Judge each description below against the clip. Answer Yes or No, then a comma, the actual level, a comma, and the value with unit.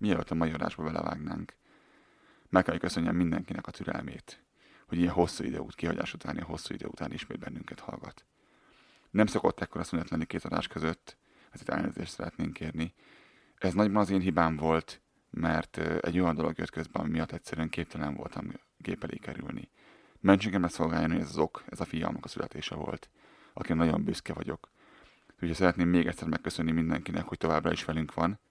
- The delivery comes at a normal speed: No, fast, 180 wpm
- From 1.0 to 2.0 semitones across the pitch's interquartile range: Yes, narrow, 1.5 semitones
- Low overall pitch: Yes, very low, 85 Hz